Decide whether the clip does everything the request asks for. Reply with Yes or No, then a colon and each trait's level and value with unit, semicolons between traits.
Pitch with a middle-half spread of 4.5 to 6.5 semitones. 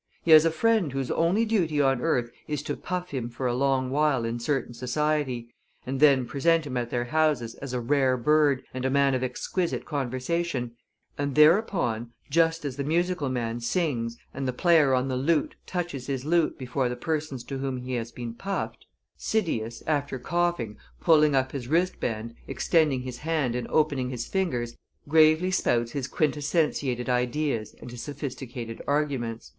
No: average, 4.0 semitones